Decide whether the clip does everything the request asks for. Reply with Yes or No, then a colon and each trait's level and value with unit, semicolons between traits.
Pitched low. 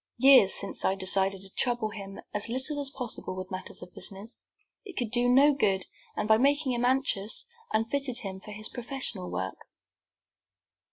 No: high, 225 Hz